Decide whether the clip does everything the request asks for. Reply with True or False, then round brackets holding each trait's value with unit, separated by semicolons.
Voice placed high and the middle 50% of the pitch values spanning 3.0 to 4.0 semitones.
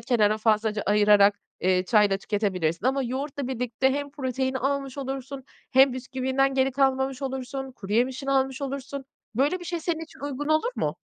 True (265 Hz; 3.4 semitones)